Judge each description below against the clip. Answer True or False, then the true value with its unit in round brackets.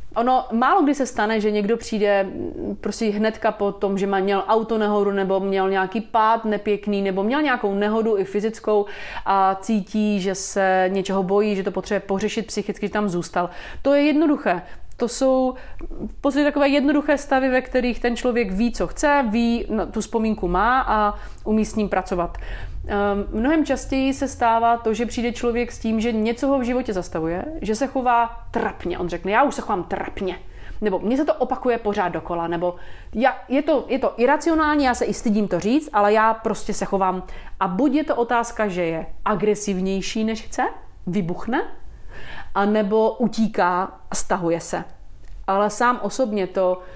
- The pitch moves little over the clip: False (4.0 semitones)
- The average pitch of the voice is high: True (215 Hz)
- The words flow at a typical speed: False (180 wpm)